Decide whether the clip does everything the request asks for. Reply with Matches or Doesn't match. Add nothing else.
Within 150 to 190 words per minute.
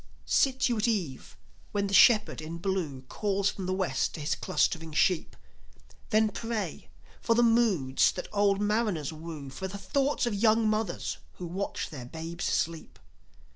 Matches